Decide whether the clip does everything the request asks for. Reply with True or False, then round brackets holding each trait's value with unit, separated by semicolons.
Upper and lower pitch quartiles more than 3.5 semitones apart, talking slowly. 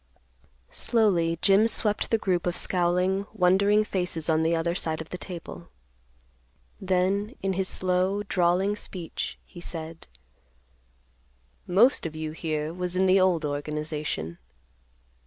False (3.0 semitones; 130 wpm)